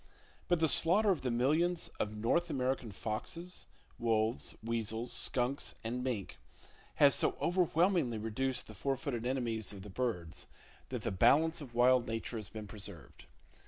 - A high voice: No, low, 120 Hz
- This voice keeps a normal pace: Yes, average, 155 wpm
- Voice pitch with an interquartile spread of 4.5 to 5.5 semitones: Yes, average, 5.2 semitones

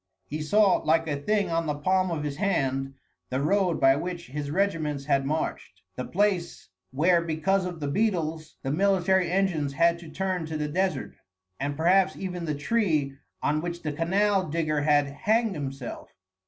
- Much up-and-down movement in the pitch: No, average, 4.3 semitones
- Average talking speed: Yes, average, 175 wpm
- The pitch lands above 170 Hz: No, medium, 165 Hz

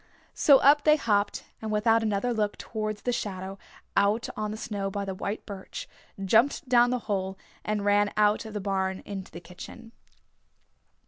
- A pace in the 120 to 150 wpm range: No, average, 175 wpm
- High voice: Yes, high, 210 Hz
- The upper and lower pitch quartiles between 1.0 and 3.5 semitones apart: Yes, narrow, 2.5 semitones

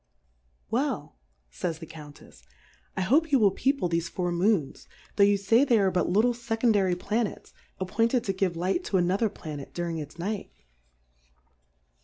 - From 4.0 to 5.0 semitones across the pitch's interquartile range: Yes, average, 4.7 semitones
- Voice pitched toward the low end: No, high, 195 Hz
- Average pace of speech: Yes, average, 160 wpm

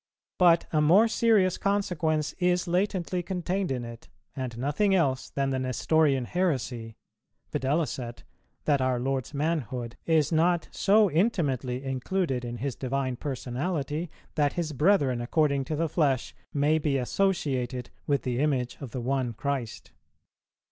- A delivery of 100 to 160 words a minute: Yes, average, 140 wpm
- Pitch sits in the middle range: Yes, medium, 145 Hz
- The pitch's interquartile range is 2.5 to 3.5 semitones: No, average, 5.0 semitones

